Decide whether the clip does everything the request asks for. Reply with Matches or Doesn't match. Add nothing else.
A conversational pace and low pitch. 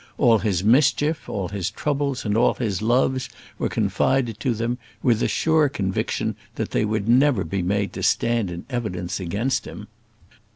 Matches